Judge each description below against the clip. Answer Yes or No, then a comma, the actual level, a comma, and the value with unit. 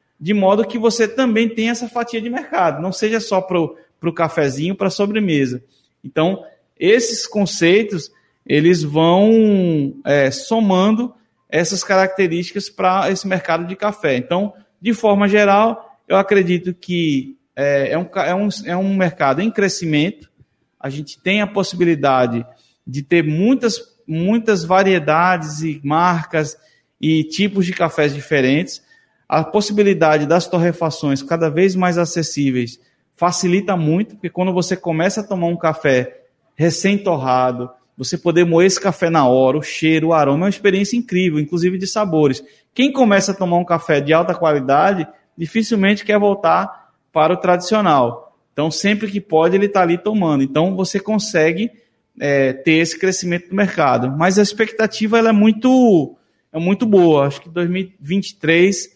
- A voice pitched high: No, medium, 180 Hz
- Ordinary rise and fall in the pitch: Yes, average, 4.3 semitones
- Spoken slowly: No, average, 150 wpm